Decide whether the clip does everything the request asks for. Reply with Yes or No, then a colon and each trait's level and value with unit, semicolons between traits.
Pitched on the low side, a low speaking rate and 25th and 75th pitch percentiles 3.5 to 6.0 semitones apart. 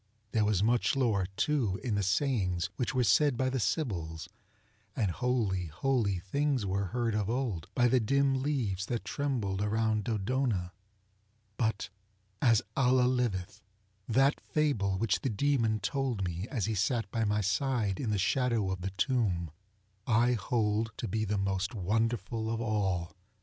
No: low, 110 Hz; average, 155 wpm; average, 4.2 semitones